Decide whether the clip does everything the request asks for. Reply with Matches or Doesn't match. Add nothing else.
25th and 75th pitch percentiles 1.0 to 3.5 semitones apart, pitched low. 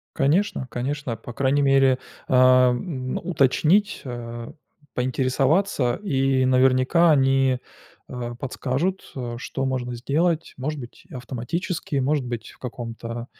Matches